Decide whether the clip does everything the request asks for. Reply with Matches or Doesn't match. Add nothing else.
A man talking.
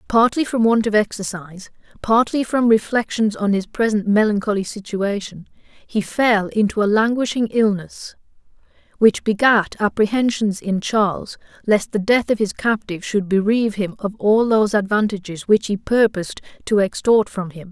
Doesn't match